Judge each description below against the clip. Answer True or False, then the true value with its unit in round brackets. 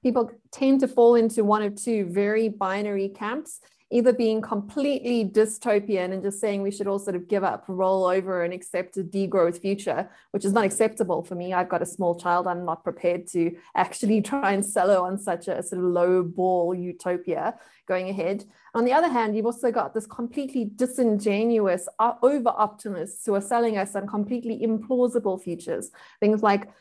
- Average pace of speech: True (190 wpm)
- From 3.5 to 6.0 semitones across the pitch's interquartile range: True (3.8 semitones)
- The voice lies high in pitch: True (205 Hz)